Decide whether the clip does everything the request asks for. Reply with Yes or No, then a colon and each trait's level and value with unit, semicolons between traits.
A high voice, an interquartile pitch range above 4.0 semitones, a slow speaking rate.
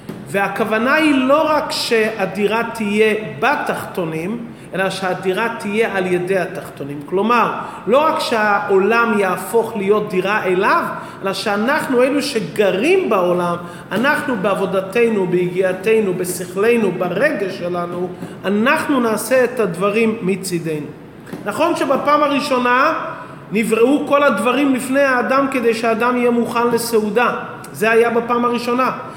Yes: high, 220 Hz; average, 4.9 semitones; slow, 110 wpm